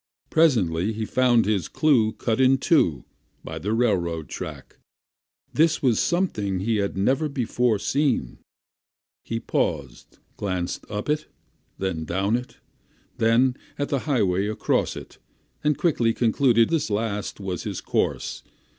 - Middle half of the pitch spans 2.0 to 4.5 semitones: No, wide, 5.4 semitones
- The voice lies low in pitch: Yes, low, 110 Hz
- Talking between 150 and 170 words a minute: No, slow, 135 wpm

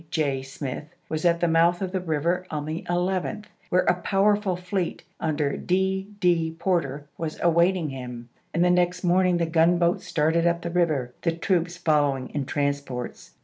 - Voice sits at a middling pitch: Yes, medium, 170 Hz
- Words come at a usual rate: Yes, average, 170 wpm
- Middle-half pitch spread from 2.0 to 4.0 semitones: Yes, average, 3.0 semitones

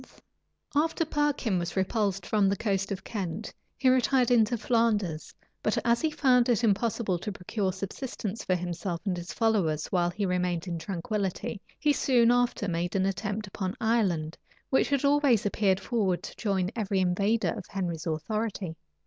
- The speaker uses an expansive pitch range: No, average, 4.3 semitones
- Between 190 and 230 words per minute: No, average, 165 wpm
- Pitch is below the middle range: No, high, 200 Hz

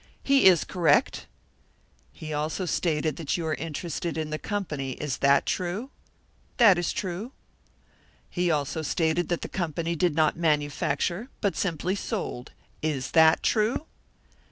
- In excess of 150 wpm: No, average, 140 wpm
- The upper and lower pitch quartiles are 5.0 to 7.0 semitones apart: No, average, 3.2 semitones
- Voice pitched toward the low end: No, medium, 165 Hz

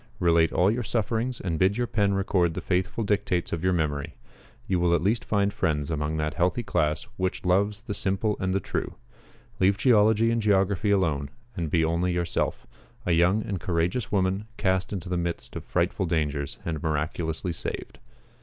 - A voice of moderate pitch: No, very low, 90 Hz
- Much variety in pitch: No, average, 3.6 semitones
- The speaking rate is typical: Yes, average, 180 wpm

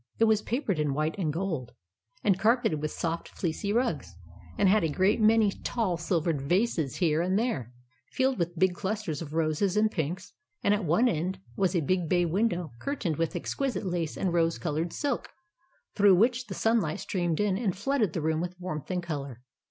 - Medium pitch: Yes, medium, 180 Hz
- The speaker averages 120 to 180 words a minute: No, average, 195 wpm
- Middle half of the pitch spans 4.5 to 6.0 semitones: Yes, average, 4.8 semitones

